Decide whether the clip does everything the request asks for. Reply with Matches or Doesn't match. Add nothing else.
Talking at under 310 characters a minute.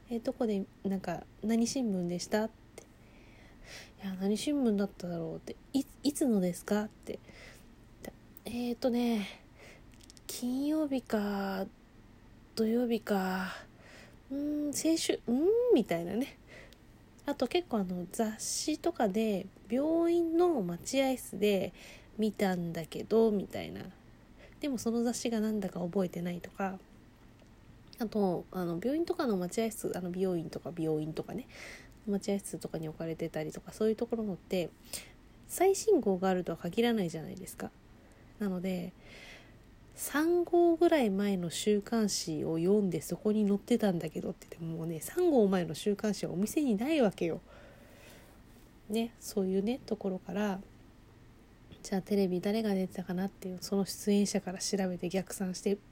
Matches